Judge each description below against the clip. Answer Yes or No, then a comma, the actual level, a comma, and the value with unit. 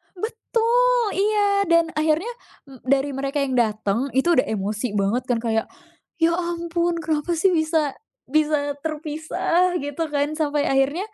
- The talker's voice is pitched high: Yes, very high, 310 Hz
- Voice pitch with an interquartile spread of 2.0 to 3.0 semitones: No, average, 4.2 semitones